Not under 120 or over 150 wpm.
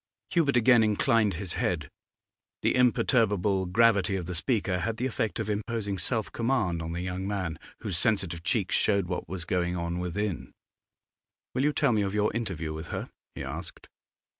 No: average, 175 wpm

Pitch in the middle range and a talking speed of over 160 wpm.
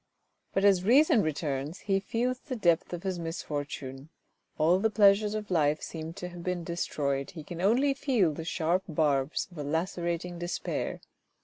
Yes: medium, 175 Hz; average, 170 wpm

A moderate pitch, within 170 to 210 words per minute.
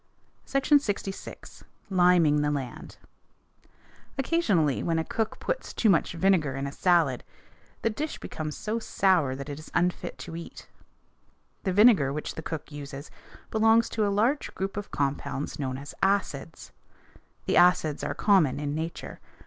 No: medium, 170 Hz; average, 150 wpm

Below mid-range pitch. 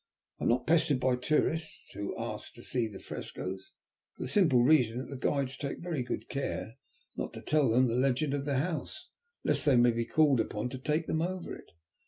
Yes: low, 130 Hz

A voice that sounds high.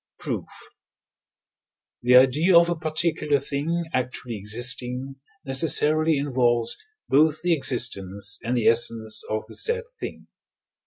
No: low, 130 Hz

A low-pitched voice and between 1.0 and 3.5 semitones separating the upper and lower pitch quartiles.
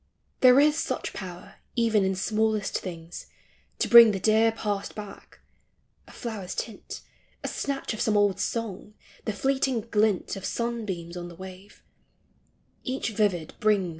No: high, 210 Hz; average, 3.1 semitones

